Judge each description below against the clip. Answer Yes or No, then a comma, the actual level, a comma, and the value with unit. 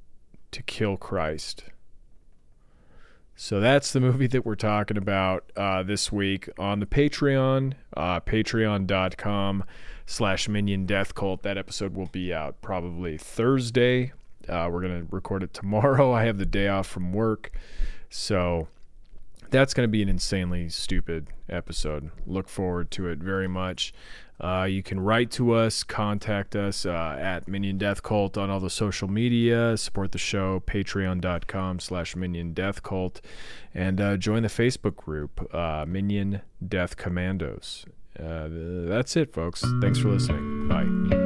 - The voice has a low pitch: Yes, very low, 95 Hz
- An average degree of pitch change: Yes, average, 3.3 semitones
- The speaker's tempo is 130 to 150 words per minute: Yes, average, 145 wpm